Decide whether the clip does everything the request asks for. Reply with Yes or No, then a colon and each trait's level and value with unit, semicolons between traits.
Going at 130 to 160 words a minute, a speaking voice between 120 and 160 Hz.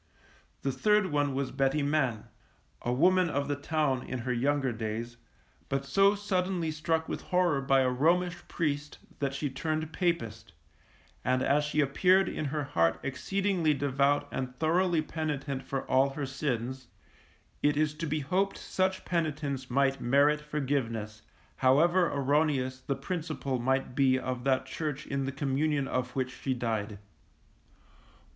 Yes: average, 150 wpm; medium, 140 Hz